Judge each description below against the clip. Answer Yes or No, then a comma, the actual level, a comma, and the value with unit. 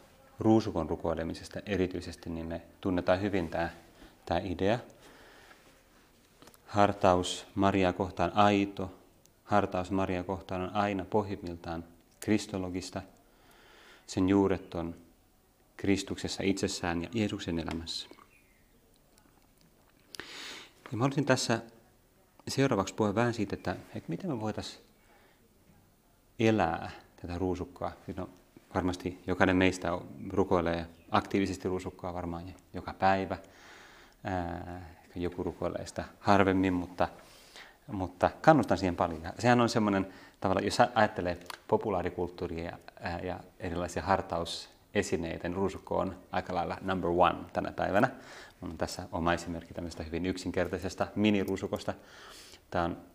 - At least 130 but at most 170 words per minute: No, average, 105 wpm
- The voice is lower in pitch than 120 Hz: Yes, very low, 95 Hz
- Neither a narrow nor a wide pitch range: No, narrow, 2.2 semitones